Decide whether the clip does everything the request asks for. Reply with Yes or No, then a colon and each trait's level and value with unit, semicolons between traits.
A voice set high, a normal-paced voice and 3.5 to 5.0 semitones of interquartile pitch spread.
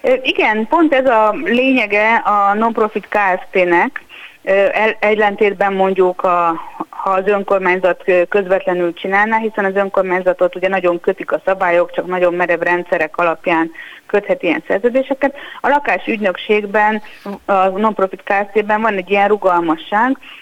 No: high, 200 Hz; average, 120 wpm; average, 2.9 semitones